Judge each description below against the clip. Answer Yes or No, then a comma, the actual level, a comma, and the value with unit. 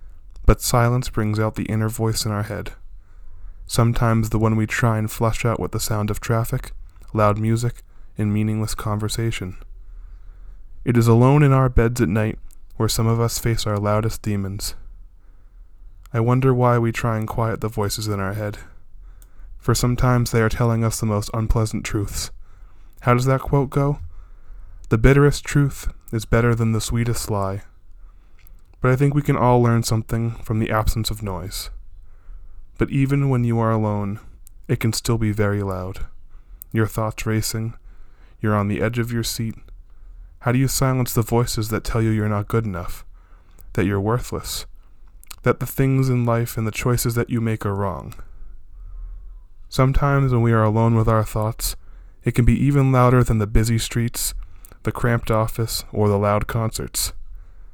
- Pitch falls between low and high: No, low, 110 Hz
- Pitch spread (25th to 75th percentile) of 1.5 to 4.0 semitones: No, average, 4.6 semitones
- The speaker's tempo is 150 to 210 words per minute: Yes, average, 175 wpm